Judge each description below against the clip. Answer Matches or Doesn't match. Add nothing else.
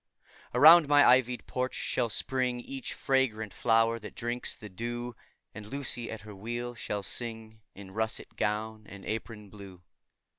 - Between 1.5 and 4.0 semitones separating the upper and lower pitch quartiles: Matches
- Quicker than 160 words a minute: Doesn't match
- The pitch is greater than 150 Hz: Doesn't match